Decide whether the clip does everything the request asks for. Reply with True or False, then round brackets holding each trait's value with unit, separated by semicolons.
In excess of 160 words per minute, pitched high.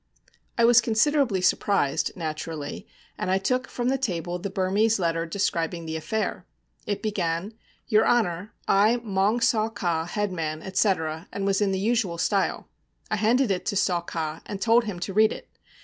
True (170 wpm; 195 Hz)